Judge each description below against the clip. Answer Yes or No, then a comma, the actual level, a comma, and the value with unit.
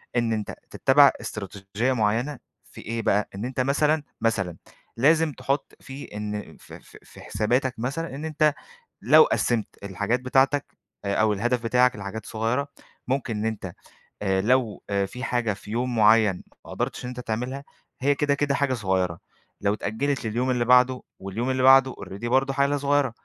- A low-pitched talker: Yes, low, 120 Hz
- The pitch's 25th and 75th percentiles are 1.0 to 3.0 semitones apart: No, average, 4.1 semitones